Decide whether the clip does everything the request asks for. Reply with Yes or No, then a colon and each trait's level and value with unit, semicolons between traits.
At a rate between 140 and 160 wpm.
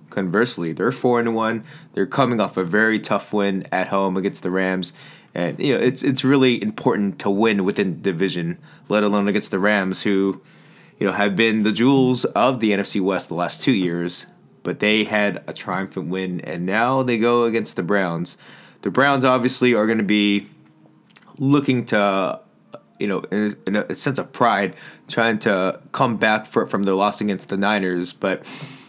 No: average, 190 wpm